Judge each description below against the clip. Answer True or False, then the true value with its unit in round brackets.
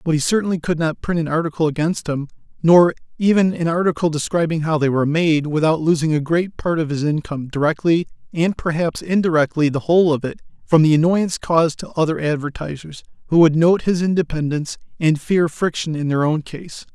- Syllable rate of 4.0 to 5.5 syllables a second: False (5.8 syllables/s)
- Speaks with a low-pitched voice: False (160 Hz)